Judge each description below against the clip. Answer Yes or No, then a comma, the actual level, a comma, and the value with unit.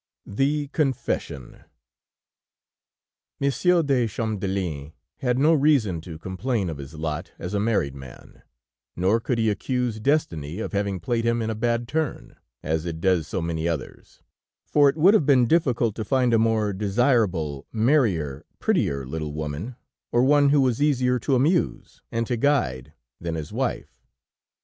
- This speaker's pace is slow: No, average, 155 wpm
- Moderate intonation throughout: No, wide, 8.0 semitones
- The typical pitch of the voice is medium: No, low, 110 Hz